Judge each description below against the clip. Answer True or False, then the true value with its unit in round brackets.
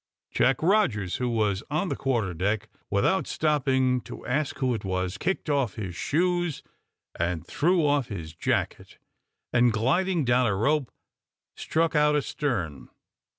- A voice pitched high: False (125 Hz)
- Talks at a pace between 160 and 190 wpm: False (145 wpm)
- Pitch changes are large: True (6.8 semitones)